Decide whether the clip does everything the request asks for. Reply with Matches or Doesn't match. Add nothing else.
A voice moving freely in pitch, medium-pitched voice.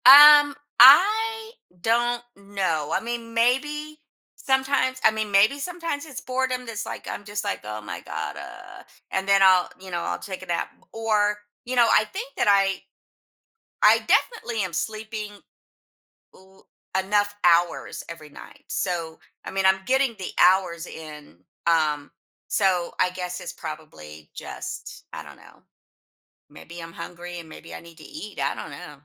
Doesn't match